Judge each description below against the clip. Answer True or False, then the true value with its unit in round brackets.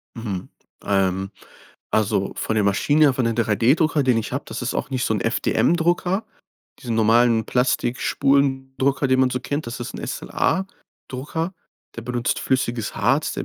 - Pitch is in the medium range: False (125 Hz)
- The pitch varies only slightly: False (3.7 semitones)